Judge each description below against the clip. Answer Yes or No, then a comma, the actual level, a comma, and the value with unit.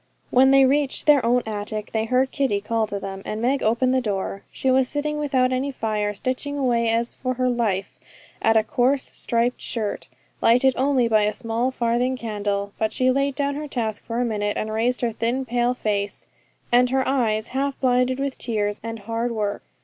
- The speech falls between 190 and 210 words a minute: Yes, average, 200 wpm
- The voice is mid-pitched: No, high, 240 Hz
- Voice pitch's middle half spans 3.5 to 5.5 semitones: No, average, 3.1 semitones